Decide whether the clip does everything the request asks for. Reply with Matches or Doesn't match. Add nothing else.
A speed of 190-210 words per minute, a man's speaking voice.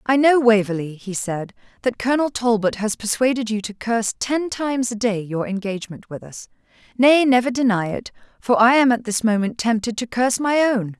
Doesn't match